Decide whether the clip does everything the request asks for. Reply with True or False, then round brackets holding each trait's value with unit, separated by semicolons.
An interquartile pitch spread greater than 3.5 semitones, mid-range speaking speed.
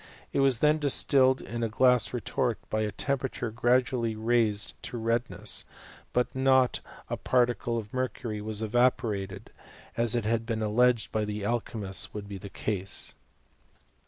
False (2.8 semitones; 155 wpm)